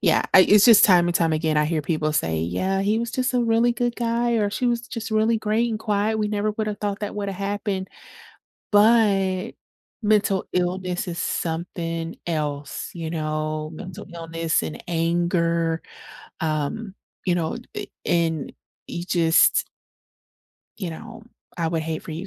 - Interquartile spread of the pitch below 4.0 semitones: No, average, 4.6 semitones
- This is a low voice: No, medium, 185 Hz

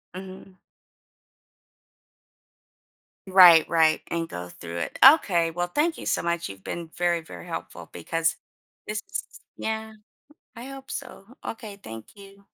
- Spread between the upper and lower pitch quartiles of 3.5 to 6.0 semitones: Yes, average, 4.4 semitones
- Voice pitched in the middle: Yes, medium, 175 Hz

